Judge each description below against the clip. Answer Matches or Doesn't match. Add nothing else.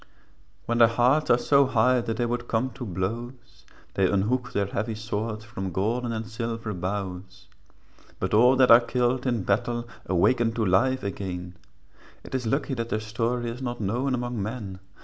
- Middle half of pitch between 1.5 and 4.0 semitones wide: Matches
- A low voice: Matches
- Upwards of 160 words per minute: Matches